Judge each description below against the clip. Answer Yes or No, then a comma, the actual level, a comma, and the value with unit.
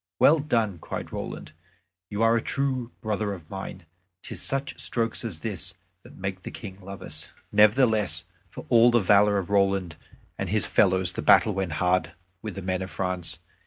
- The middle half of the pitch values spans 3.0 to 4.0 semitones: Yes, average, 3.6 semitones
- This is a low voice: Yes, low, 100 Hz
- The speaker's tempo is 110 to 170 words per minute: No, average, 180 wpm